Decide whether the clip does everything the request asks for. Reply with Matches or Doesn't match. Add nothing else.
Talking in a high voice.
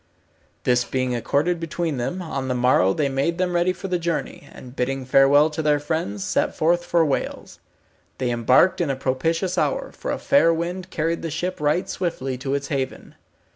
Doesn't match